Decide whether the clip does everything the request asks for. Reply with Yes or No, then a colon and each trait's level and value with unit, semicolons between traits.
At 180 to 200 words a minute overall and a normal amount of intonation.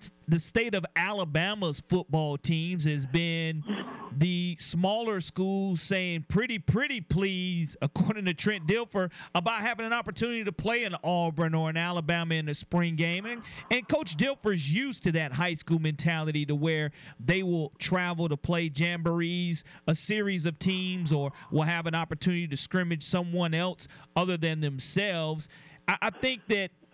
No: average, 160 wpm; average, 3.2 semitones